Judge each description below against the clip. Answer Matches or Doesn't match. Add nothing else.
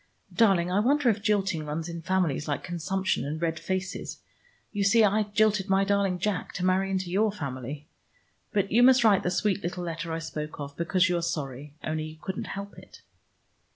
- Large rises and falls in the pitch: Doesn't match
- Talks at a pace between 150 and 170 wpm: Doesn't match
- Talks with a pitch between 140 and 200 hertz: Matches